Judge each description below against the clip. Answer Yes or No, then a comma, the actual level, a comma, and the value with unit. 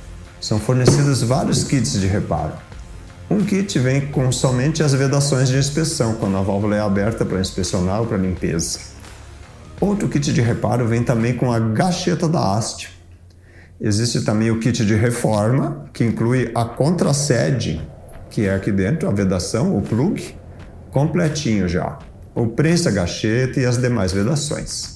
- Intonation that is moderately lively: No, wide, 5.9 semitones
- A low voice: Yes, low, 115 Hz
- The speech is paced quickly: No, average, 150 wpm